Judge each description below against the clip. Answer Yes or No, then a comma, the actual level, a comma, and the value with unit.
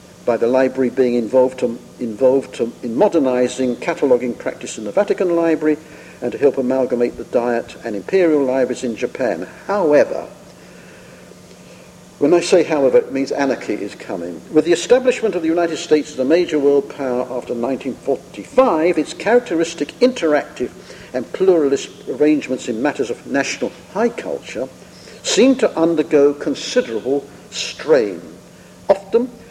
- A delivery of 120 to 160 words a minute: Yes, average, 140 wpm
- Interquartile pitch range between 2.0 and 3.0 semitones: No, average, 5.1 semitones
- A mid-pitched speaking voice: Yes, medium, 150 Hz